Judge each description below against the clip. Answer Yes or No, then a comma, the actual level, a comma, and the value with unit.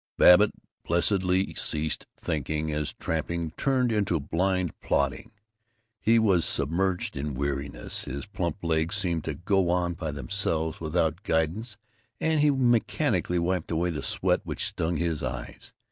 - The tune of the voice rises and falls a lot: No, average, 3.7 semitones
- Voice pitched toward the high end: No, very low, 85 Hz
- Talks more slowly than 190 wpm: Yes, average, 140 wpm